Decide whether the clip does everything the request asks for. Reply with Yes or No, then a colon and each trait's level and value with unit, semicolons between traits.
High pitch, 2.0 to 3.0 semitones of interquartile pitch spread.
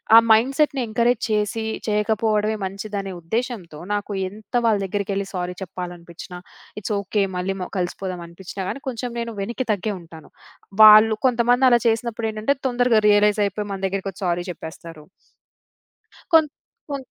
No: high, 210 Hz; average, 3.5 semitones